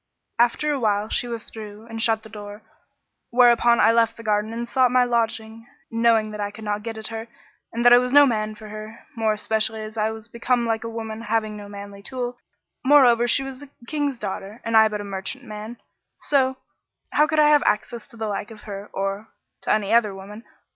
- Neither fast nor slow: No, fast, 215 wpm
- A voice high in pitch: Yes, high, 225 Hz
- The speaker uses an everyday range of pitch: No, narrow, 2.0 semitones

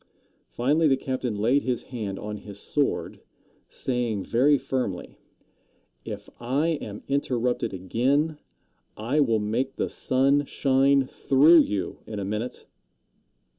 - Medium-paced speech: No, slow, 125 wpm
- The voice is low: Yes, low, 125 Hz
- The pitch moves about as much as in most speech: Yes, average, 4.4 semitones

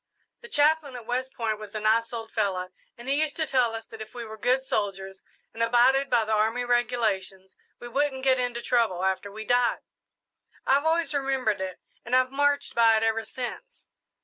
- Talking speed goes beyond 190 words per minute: Yes, average, 200 wpm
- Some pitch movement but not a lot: Yes, average, 3.4 semitones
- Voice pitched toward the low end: No, high, 240 Hz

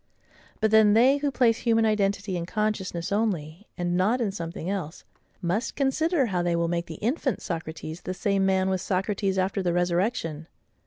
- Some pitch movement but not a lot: Yes, average, 3.9 semitones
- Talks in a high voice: Yes, high, 195 Hz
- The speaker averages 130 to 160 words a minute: No, average, 175 wpm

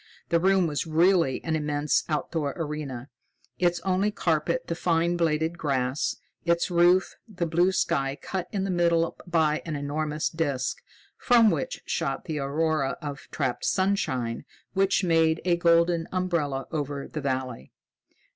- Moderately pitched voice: Yes, medium, 165 Hz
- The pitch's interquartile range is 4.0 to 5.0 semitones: No, average, 3.2 semitones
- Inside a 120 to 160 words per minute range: Yes, average, 145 wpm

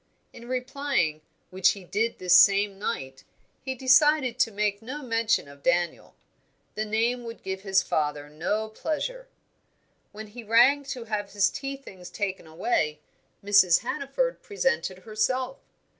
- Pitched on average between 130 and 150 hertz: No, high, 215 Hz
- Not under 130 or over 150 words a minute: Yes, average, 145 wpm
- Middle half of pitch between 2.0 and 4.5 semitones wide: No, average, 5.3 semitones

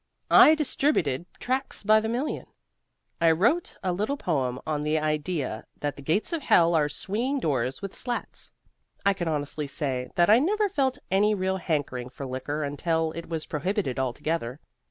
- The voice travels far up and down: Yes, wide, 6.8 semitones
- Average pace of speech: Yes, average, 170 wpm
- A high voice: No, medium, 165 Hz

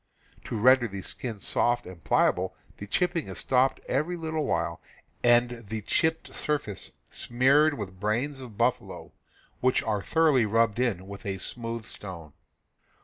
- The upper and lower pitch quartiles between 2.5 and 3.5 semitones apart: No, average, 4.8 semitones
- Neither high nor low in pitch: No, low, 120 Hz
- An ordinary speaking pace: Yes, average, 150 wpm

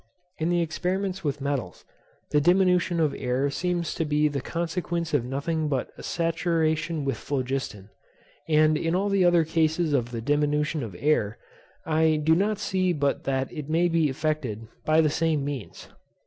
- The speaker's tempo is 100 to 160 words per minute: No, average, 170 wpm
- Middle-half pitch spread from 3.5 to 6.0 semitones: No, average, 3.1 semitones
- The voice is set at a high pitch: No, medium, 155 Hz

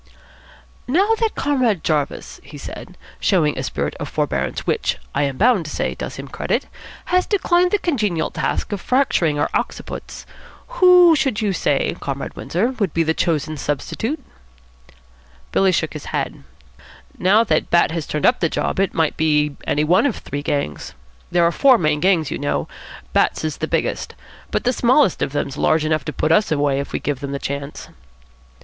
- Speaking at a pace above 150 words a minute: Yes, average, 185 wpm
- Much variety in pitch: Yes, wide, 8.3 semitones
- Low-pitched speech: No, medium, 165 Hz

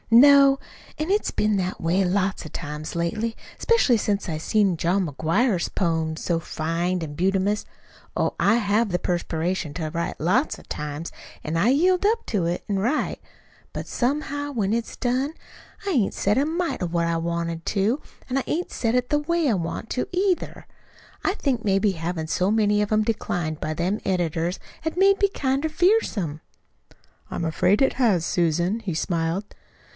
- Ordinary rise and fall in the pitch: No, wide, 7.4 semitones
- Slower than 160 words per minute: No, average, 175 wpm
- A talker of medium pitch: No, high, 200 Hz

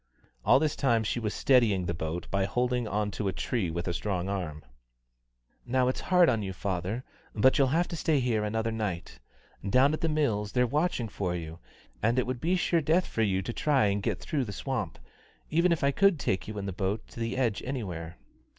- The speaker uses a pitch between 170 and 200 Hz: No, low, 115 Hz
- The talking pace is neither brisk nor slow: No, fast, 220 wpm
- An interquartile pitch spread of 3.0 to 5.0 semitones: No, wide, 5.6 semitones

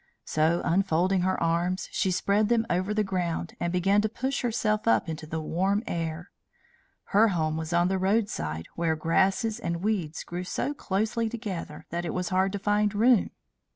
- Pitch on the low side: No, medium, 185 Hz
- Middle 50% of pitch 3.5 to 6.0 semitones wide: Yes, average, 3.8 semitones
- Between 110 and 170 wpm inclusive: No, average, 180 wpm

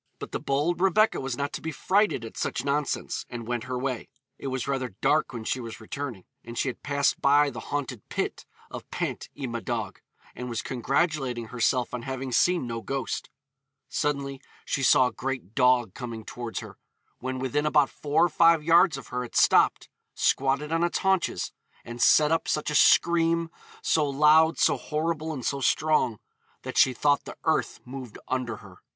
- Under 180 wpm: No, average, 185 wpm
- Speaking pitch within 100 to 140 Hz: Yes, low, 135 Hz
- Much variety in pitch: No, average, 3.6 semitones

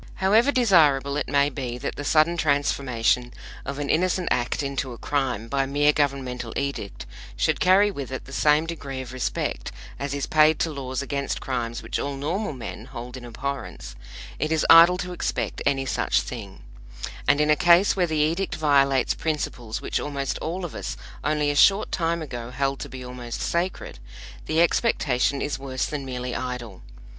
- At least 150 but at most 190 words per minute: Yes, average, 180 wpm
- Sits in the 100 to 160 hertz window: Yes, medium, 140 Hz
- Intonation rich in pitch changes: No, average, 3.6 semitones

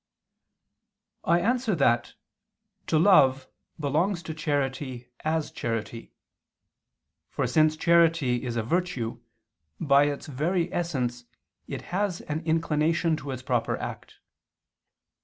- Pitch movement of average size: Yes, average, 4.6 semitones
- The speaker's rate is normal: No, slow, 110 wpm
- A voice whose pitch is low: No, medium, 150 Hz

